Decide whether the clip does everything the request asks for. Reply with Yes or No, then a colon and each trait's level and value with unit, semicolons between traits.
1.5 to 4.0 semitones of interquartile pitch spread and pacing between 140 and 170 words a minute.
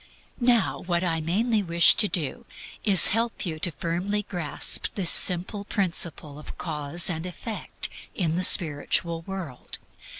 Yes: average, 3.5 semitones; average, 145 wpm